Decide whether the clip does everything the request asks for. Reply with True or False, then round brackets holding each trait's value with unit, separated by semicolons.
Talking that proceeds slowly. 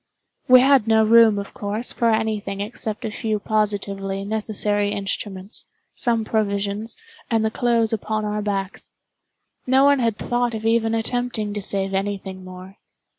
False (160 wpm)